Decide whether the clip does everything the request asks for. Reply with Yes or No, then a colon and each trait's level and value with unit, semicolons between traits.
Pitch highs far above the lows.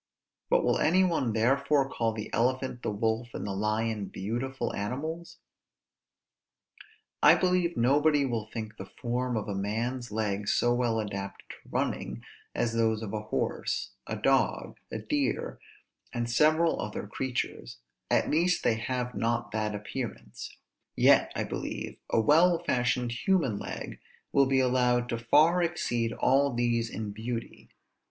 No: average, 3.5 semitones